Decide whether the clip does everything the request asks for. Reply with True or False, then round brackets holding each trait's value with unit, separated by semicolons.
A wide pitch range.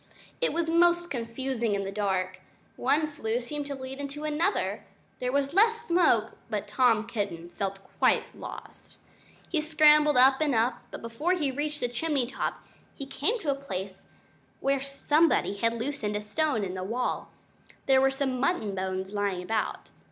True (6.1 semitones)